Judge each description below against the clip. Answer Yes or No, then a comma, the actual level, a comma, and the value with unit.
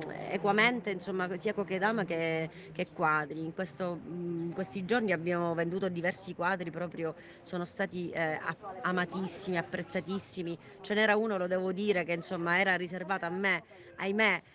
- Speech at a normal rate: Yes, average, 145 wpm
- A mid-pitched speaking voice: Yes, medium, 180 Hz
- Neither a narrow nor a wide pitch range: No, narrow, 2.2 semitones